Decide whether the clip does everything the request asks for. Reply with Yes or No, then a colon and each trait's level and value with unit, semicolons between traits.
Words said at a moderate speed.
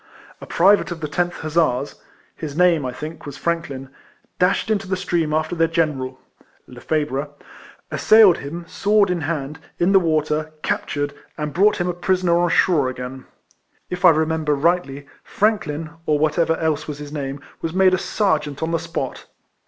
Yes: average, 175 wpm